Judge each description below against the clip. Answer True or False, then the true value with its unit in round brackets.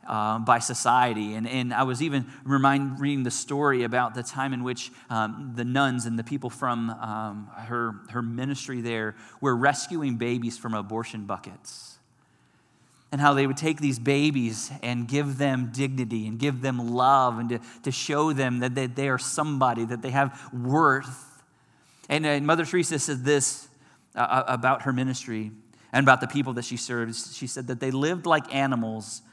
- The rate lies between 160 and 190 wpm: True (180 wpm)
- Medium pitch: False (130 Hz)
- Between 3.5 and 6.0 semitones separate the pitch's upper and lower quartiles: False (2.8 semitones)